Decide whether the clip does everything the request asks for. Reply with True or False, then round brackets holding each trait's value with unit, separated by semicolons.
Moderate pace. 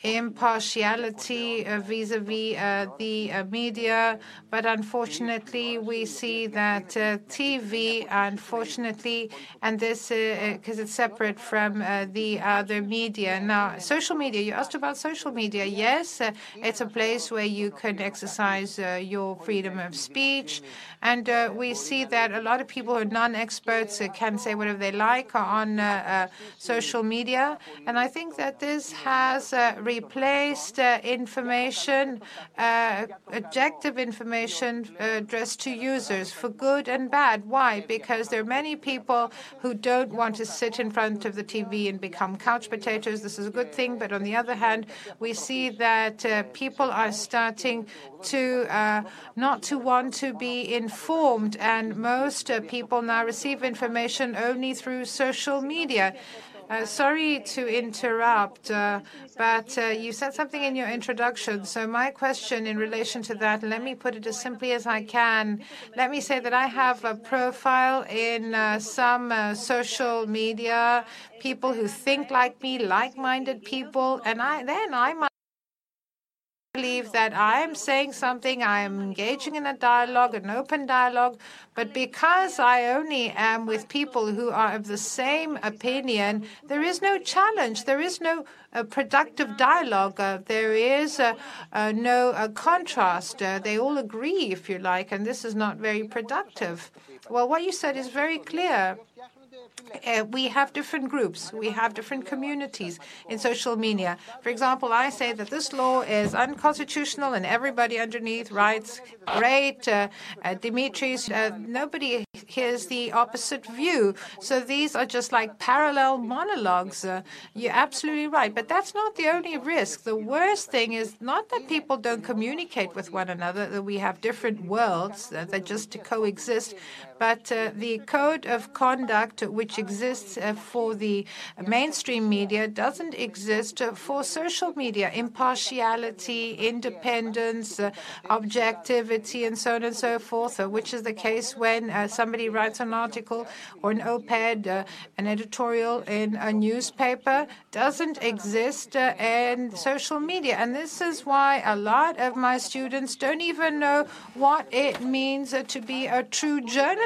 True (160 wpm)